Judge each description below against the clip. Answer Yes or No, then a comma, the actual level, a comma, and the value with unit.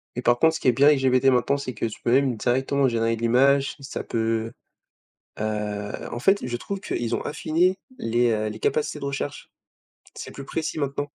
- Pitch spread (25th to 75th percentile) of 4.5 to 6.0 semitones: No, average, 3.4 semitones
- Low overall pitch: Yes, low, 130 Hz